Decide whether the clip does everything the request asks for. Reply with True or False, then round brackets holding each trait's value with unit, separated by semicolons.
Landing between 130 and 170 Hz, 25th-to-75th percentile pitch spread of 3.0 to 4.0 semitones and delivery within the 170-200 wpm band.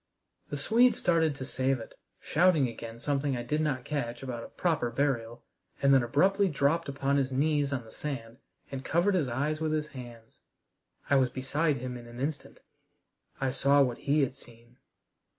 True (140 Hz; 3.5 semitones; 185 wpm)